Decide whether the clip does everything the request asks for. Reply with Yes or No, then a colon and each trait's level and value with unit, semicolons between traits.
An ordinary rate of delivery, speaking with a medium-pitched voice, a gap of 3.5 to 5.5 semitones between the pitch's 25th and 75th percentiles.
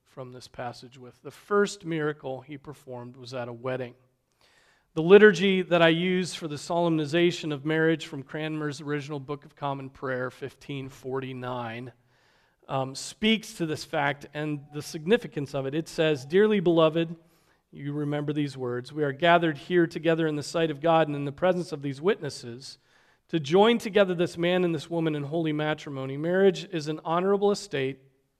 Yes: average, 175 wpm; medium, 150 Hz; average, 4.1 semitones